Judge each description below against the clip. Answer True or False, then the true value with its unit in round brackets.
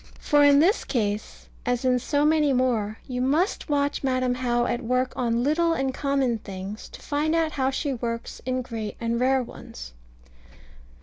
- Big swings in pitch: False (3.5 semitones)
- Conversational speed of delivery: True (175 wpm)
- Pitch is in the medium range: False (255 Hz)